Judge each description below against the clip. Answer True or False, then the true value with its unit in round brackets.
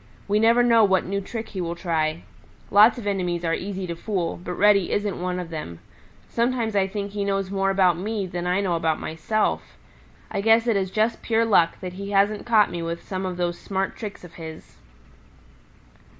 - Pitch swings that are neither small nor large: True (3.1 semitones)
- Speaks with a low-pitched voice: False (195 Hz)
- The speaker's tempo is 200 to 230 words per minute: True (205 wpm)